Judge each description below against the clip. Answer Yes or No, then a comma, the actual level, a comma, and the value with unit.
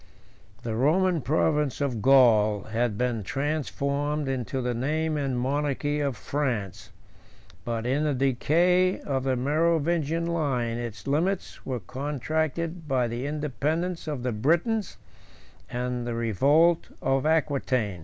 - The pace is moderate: No, slow, 125 wpm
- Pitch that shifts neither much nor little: Yes, average, 4.1 semitones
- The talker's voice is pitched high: No, medium, 140 Hz